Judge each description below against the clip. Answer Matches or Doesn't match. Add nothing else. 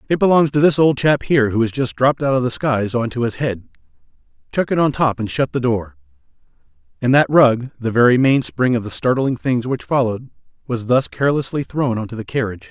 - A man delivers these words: Matches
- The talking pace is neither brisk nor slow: Doesn't match